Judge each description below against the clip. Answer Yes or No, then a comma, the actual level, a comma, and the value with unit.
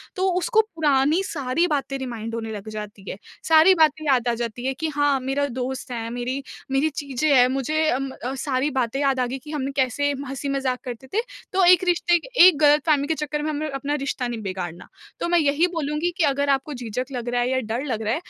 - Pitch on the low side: No, very high, 275 Hz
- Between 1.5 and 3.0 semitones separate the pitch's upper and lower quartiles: No, average, 3.7 semitones